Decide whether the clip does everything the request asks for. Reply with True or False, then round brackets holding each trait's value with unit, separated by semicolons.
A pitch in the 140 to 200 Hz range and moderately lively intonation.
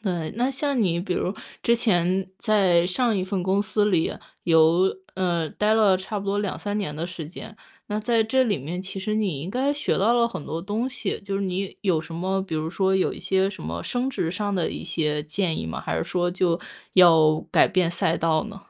True (190 Hz; 3.7 semitones)